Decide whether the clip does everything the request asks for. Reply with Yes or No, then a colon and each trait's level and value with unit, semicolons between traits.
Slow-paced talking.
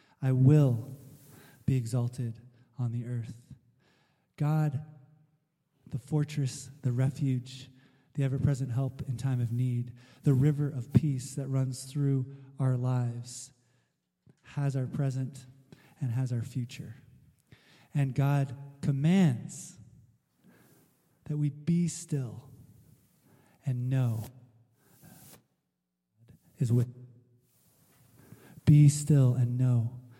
Yes: slow, 105 wpm